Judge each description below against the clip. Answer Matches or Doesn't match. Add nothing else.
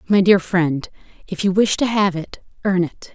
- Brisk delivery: Matches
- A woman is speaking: Matches